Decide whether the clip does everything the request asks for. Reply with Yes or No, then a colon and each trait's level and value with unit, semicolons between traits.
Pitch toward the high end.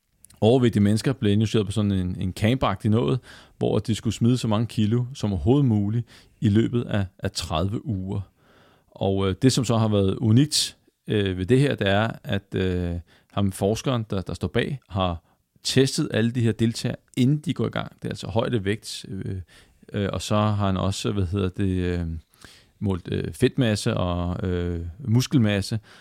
No: low, 105 Hz